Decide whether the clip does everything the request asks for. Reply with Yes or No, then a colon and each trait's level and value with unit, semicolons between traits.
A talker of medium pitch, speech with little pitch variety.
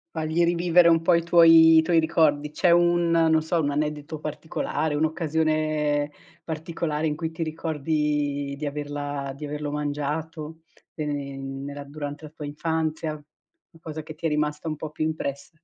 Yes: medium, 155 Hz; narrow, 1.7 semitones